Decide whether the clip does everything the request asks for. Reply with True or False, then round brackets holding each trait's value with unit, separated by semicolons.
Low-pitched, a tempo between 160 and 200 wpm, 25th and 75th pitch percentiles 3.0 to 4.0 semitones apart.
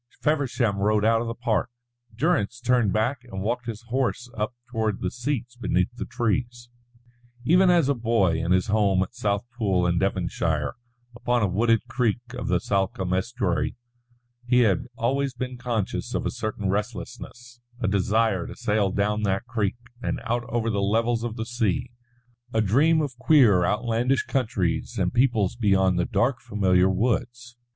True (115 Hz; 165 wpm; 3.7 semitones)